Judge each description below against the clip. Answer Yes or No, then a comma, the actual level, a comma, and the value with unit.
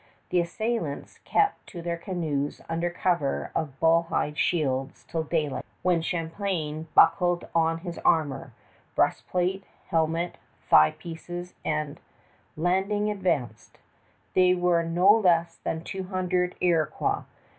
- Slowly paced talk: Yes, slow, 120 wpm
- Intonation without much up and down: Yes, narrow, 2.2 semitones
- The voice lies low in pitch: No, medium, 170 Hz